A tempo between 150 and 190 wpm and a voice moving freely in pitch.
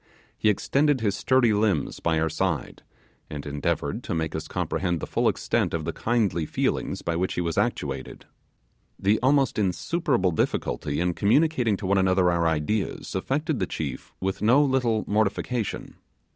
Yes: average, 160 wpm; wide, 6.1 semitones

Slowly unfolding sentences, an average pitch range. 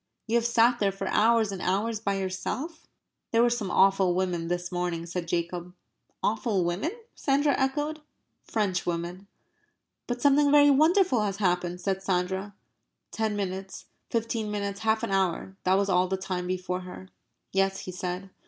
No: average, 160 wpm; average, 3.9 semitones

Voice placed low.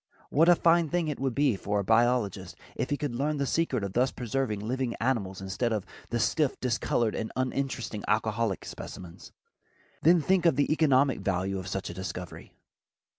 Yes: low, 120 Hz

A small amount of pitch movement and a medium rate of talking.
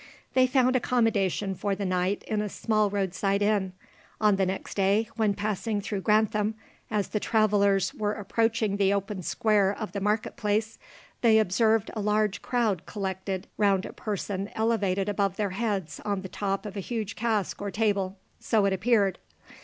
Yes: narrow, 1.9 semitones; average, 170 wpm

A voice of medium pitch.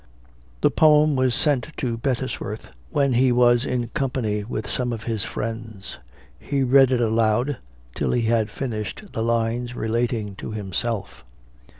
No: low, 120 Hz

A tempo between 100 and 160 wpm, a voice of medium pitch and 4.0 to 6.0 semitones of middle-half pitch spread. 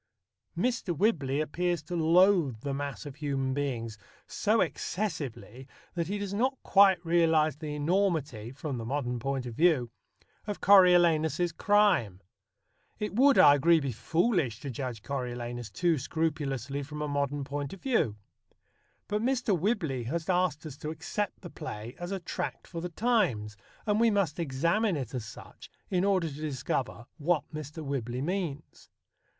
Yes: average, 155 wpm; medium, 155 Hz; average, 5.3 semitones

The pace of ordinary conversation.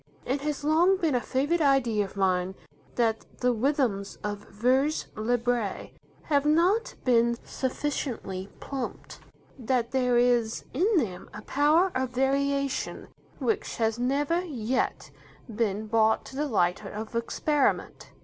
No: slow, 130 wpm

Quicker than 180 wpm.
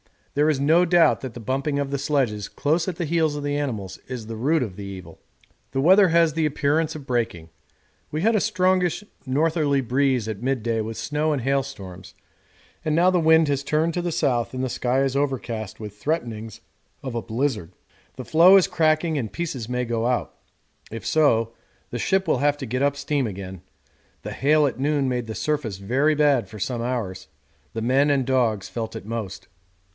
Yes: average, 200 wpm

